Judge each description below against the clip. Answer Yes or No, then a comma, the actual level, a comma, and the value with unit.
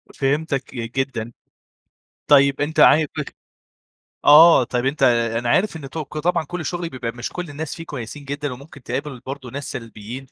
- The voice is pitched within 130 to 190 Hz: Yes, medium, 140 Hz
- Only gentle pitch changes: No, average, 3.7 semitones